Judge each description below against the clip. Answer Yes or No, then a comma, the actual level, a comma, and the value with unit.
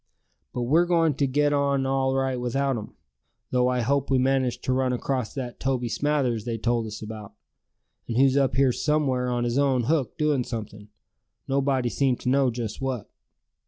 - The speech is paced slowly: No, average, 185 wpm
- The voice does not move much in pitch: Yes, narrow, 2.3 semitones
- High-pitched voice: No, low, 130 Hz